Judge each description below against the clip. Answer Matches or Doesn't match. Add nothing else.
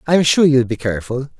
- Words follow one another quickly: Matches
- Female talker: Doesn't match